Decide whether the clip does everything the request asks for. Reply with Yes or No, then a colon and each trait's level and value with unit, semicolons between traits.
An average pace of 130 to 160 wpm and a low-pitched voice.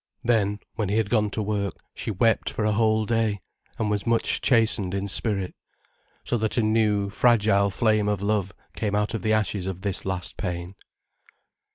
No: average, 185 wpm; low, 105 Hz